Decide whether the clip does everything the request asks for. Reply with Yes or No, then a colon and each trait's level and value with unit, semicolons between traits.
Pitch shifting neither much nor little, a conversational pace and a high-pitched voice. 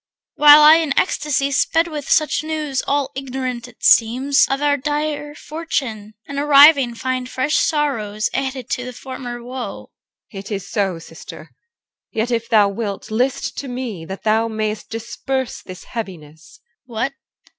Yes: average, 4.6 semitones; average, 155 wpm; very high, 255 Hz